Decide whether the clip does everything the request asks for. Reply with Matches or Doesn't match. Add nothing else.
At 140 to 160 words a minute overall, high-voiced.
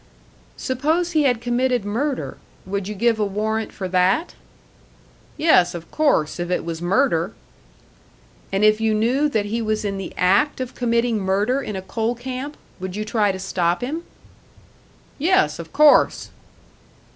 Matches